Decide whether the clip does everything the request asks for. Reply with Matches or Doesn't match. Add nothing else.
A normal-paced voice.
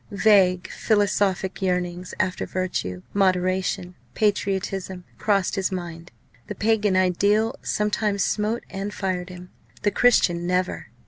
Doesn't match